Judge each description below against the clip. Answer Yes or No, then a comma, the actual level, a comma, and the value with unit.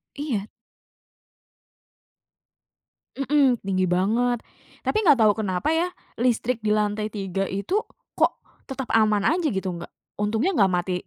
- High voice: Yes, high, 215 Hz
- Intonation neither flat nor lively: Yes, average, 5.0 semitones